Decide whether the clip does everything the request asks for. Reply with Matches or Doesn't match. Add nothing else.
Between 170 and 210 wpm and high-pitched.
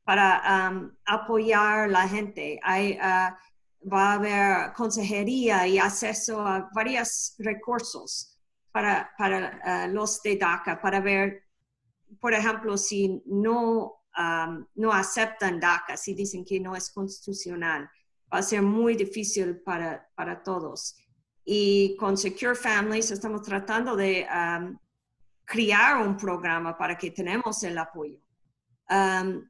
Doesn't match